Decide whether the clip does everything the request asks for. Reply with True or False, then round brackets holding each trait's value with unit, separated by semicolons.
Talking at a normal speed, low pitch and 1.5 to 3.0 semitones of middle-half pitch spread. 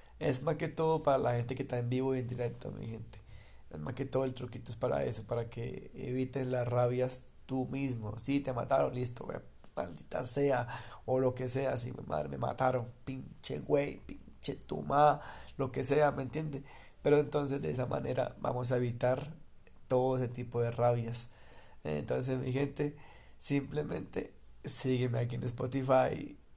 True (175 wpm; 130 Hz; 2.4 semitones)